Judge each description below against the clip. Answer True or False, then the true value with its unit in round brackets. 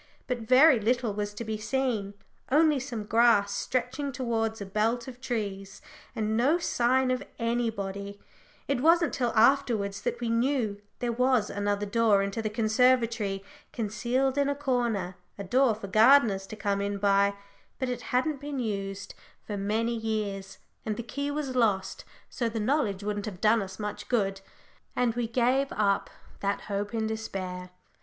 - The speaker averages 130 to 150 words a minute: False (165 wpm)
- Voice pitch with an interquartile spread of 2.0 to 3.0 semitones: False (3.7 semitones)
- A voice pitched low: False (225 Hz)